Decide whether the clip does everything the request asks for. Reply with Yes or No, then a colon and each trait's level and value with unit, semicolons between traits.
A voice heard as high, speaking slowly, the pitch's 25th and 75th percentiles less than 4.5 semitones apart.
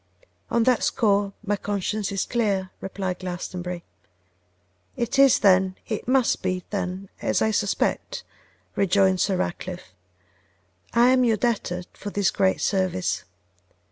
Yes: high, 195 Hz; slow, 130 wpm; average, 2.9 semitones